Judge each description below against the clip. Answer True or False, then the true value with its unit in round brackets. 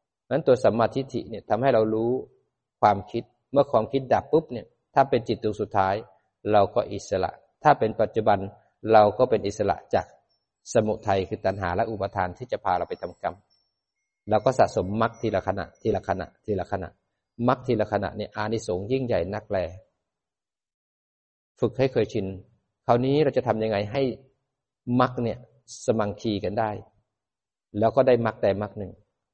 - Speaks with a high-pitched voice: False (110 Hz)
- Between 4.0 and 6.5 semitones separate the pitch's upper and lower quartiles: False (3.2 semitones)